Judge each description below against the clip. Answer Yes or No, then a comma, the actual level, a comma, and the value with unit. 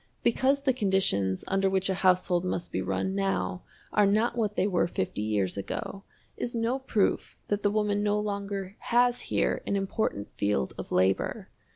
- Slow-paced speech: No, average, 175 wpm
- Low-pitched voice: No, high, 195 Hz